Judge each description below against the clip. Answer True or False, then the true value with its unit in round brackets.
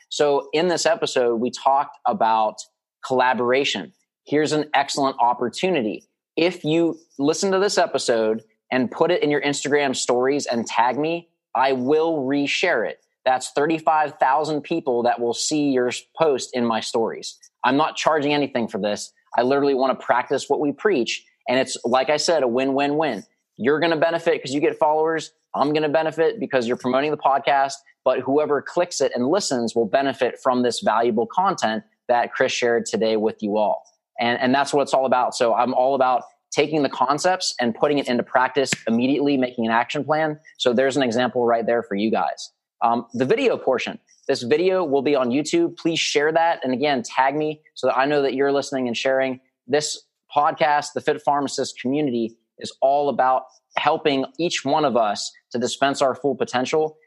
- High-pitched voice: False (140 Hz)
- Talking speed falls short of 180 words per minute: False (190 wpm)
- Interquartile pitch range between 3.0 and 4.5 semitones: True (3.6 semitones)